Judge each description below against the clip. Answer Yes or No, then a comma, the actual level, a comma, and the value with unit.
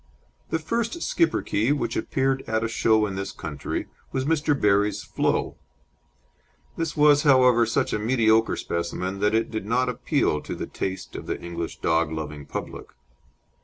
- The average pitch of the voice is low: Yes, low, 115 Hz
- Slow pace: No, average, 160 wpm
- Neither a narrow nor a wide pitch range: No, wide, 5.7 semitones